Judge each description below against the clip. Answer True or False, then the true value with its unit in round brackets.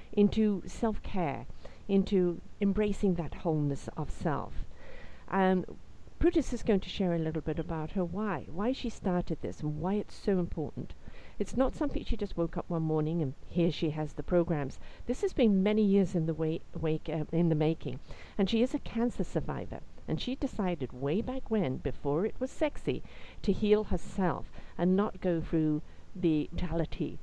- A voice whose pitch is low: False (180 Hz)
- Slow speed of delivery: False (185 wpm)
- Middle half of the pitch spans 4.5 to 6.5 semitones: True (4.8 semitones)